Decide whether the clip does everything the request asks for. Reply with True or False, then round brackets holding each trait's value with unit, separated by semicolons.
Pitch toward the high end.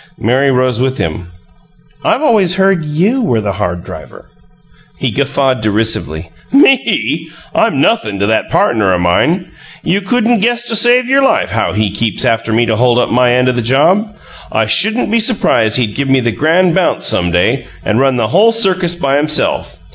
False (135 Hz)